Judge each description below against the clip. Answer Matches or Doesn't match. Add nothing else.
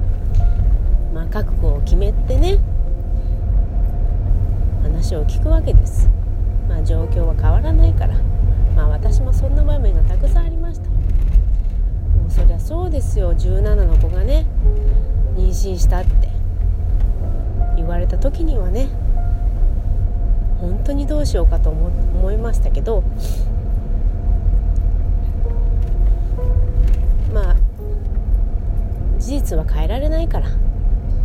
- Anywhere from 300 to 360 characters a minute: Doesn't match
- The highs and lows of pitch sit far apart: Doesn't match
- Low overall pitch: Matches